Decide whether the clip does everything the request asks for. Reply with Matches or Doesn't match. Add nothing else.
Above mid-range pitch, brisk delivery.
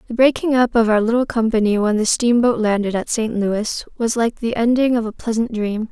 Matches